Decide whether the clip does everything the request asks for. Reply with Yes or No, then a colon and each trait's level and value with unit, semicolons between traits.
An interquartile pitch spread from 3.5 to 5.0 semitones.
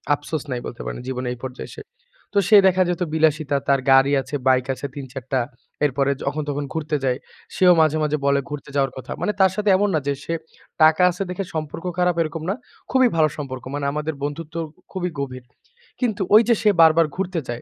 Yes: average, 4.3 semitones